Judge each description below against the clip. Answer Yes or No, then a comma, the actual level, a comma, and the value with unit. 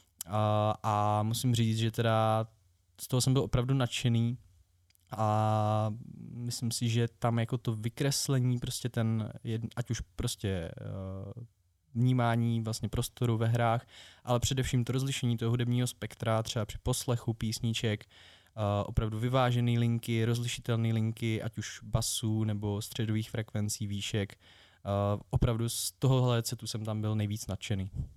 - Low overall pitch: Yes, low, 115 Hz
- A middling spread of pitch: No, narrow, 2.2 semitones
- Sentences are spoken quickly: No, average, 140 wpm